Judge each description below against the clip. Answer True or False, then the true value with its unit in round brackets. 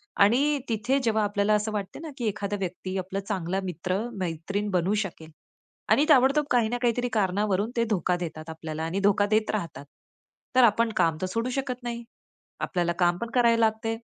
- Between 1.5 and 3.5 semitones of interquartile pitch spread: False (4.2 semitones)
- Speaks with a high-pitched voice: True (210 Hz)